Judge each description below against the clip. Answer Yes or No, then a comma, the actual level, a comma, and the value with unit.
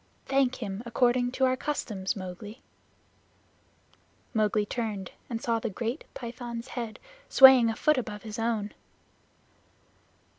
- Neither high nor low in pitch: No, high, 230 Hz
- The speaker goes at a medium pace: No, slow, 120 wpm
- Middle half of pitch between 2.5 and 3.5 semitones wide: Yes, average, 2.9 semitones